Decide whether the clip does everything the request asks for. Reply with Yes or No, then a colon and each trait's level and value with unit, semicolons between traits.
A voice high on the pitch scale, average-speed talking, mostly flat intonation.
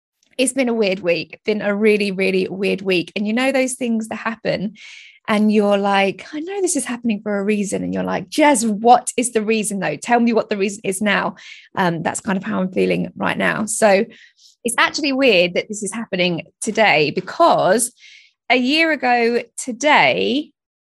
No: high, 220 Hz; average, 195 wpm; average, 4.6 semitones